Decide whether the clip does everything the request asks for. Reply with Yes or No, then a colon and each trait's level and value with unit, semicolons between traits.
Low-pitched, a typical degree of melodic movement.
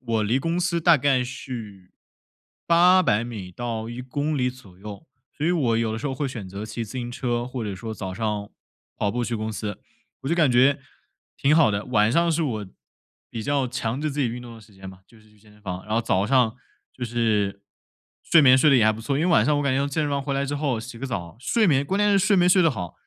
Yes: low, 120 Hz; average, 4.9 semitones